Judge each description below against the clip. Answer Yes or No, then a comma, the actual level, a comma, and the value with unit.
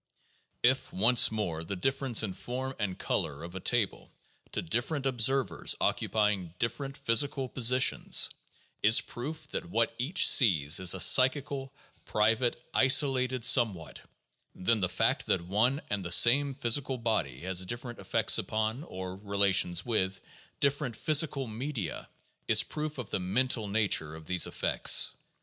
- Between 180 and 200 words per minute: No, average, 145 wpm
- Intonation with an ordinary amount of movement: No, wide, 5.8 semitones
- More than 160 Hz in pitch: No, low, 115 Hz